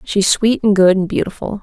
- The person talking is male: No, female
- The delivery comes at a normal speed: No, fast, 220 wpm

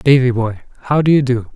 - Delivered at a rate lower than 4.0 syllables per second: No, 6.1 syllables/s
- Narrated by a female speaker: No, male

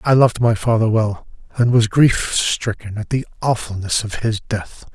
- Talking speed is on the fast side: No, average, 180 wpm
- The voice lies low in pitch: Yes, low, 110 Hz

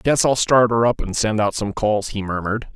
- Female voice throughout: No, male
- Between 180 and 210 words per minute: No, fast, 260 wpm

